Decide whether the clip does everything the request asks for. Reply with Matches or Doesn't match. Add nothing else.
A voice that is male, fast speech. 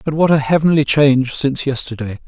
Doesn't match